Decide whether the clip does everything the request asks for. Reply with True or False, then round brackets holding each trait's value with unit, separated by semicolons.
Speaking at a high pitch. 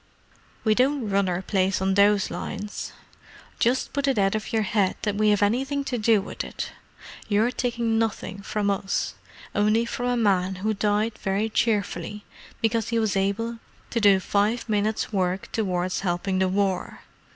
True (210 Hz)